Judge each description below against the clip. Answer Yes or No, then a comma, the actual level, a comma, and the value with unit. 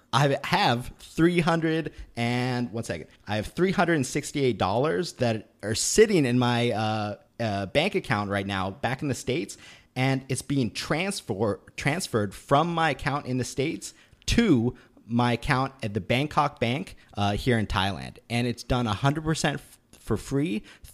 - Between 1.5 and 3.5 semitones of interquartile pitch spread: No, average, 4.3 semitones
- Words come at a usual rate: Yes, average, 165 wpm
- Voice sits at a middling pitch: No, low, 125 Hz